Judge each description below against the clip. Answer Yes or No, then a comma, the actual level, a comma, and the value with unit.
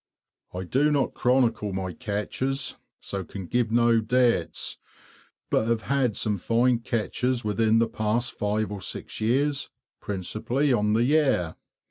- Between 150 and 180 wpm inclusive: No, average, 140 wpm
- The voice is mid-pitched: No, low, 115 Hz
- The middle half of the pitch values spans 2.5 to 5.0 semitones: Yes, average, 3.4 semitones